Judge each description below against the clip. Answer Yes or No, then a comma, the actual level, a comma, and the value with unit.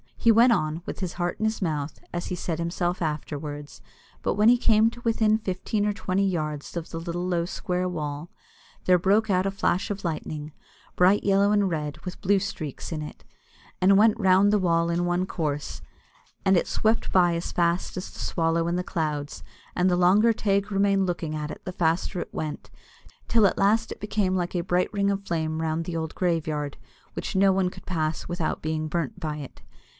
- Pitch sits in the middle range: Yes, medium, 180 Hz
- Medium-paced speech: No, fast, 210 wpm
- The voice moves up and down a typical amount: Yes, average, 3.6 semitones